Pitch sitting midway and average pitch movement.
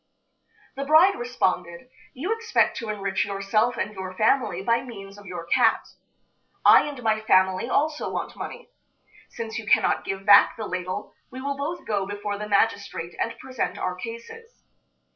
No: high, 215 Hz; average, 4.7 semitones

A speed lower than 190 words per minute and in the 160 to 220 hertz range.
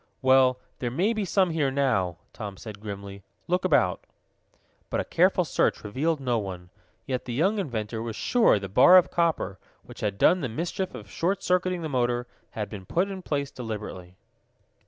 No: average, 180 wpm; low, 130 Hz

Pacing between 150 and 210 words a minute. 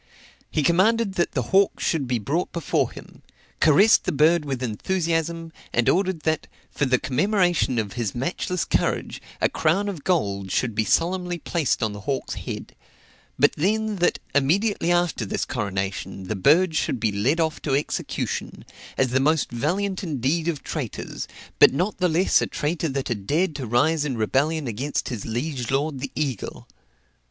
Yes: average, 170 wpm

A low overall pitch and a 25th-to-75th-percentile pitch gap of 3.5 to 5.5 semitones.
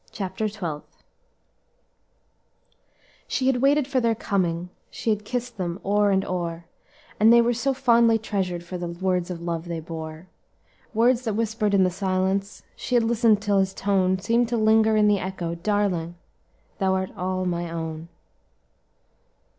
No: high, 195 Hz; average, 4.2 semitones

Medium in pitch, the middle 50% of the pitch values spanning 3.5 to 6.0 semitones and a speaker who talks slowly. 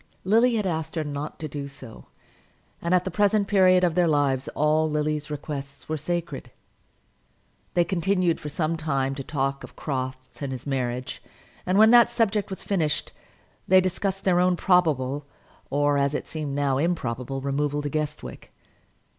No: medium, 155 Hz; average, 4.5 semitones; average, 165 wpm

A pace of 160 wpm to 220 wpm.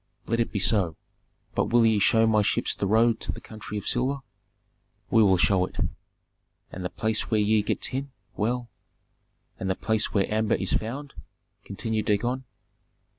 Yes: average, 180 wpm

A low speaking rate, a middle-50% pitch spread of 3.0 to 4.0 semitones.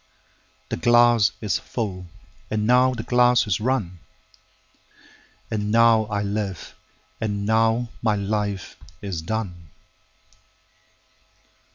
Yes: slow, 95 wpm; average, 3.7 semitones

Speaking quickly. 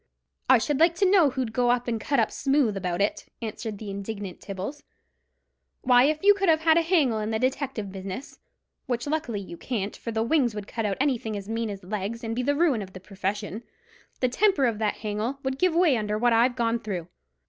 Yes: fast, 210 wpm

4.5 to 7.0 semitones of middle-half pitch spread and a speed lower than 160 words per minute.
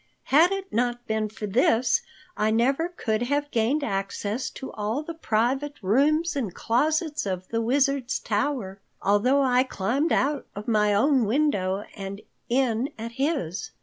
Yes: average, 5.1 semitones; average, 150 wpm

